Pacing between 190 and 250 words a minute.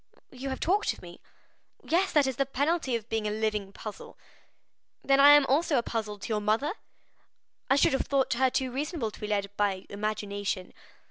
Yes: average, 195 wpm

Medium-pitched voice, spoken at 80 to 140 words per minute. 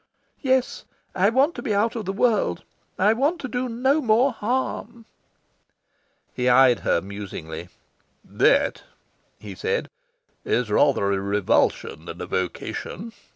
No: high, 205 Hz; slow, 135 wpm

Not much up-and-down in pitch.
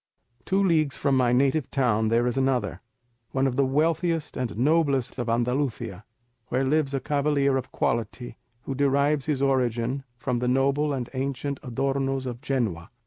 Yes: narrow, 2.3 semitones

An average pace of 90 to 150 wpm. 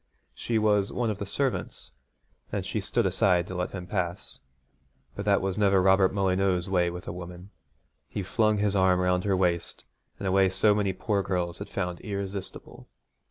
No: average, 185 wpm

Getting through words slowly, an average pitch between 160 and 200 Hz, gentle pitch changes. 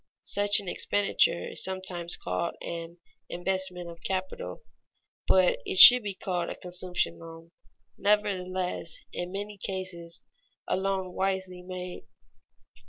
Yes: slow, 120 wpm; medium, 185 Hz; narrow, 1.5 semitones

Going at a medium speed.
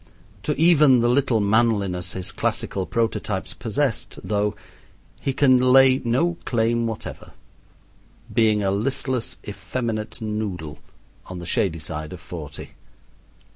No: slow, 120 wpm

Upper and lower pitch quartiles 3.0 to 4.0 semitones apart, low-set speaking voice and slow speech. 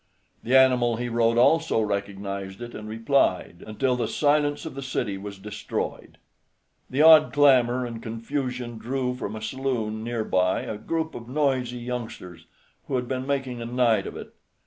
No: average, 3.3 semitones; low, 120 Hz; average, 170 wpm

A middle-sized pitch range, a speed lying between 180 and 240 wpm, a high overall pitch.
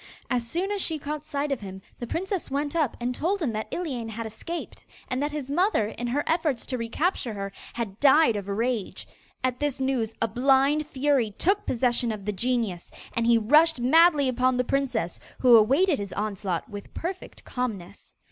Yes: average, 5.0 semitones; average, 190 wpm; very high, 255 Hz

